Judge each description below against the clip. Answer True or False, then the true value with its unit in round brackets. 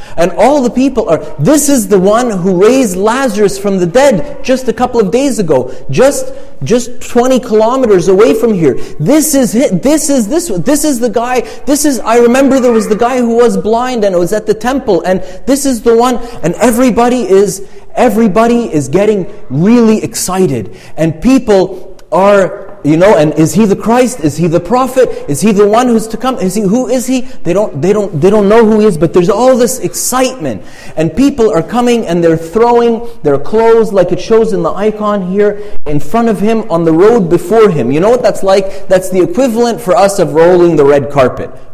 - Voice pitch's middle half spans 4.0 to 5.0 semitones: True (4.7 semitones)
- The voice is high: True (220 Hz)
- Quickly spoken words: True (210 wpm)